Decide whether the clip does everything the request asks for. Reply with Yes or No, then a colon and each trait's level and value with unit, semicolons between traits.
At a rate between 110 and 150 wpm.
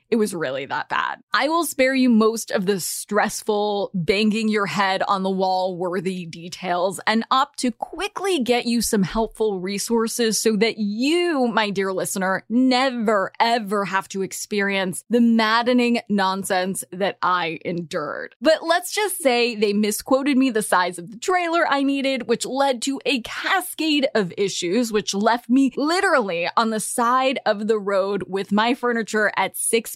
No: average, 165 wpm